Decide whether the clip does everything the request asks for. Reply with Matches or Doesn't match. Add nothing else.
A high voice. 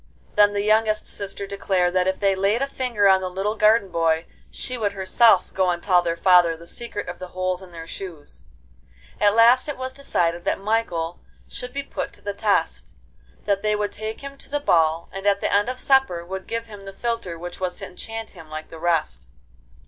Matches